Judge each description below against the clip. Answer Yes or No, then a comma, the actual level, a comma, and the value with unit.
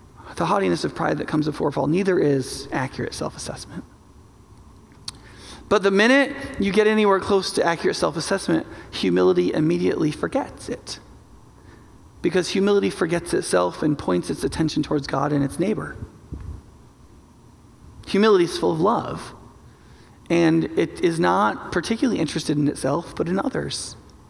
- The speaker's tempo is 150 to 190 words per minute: No, average, 140 wpm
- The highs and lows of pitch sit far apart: Yes, wide, 8.2 semitones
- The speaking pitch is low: No, medium, 155 Hz